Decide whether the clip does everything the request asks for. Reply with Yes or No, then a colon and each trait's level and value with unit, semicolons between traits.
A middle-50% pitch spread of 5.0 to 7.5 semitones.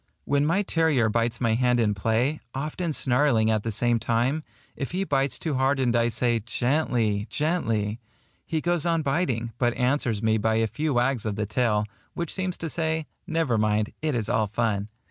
Yes: wide, 5.5 semitones